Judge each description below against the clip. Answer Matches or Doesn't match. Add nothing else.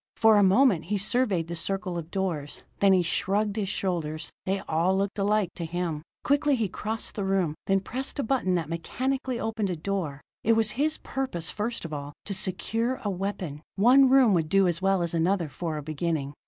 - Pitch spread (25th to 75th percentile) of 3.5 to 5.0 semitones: Matches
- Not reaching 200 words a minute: Doesn't match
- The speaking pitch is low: Doesn't match